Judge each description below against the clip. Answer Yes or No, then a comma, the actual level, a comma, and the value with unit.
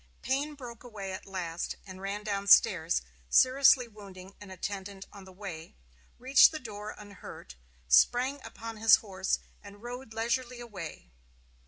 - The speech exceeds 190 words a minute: No, average, 145 wpm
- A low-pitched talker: No, high, 205 Hz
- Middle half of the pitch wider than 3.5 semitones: Yes, average, 4.0 semitones